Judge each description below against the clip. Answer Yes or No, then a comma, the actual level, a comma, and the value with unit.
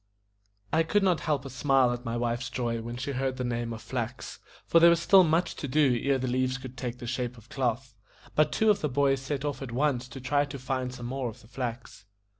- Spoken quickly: Yes, fast, 245 wpm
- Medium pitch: No, low, 130 Hz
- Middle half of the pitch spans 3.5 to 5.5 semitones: No, average, 2.7 semitones